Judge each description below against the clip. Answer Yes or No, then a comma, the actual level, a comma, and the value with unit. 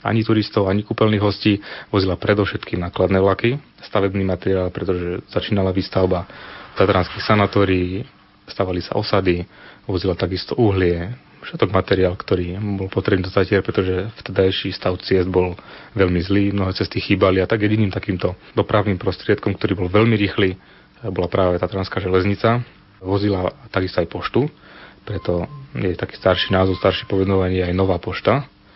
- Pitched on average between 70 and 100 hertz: Yes, very low, 95 Hz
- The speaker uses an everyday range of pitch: No, narrow, 2.0 semitones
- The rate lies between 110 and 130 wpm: No, average, 140 wpm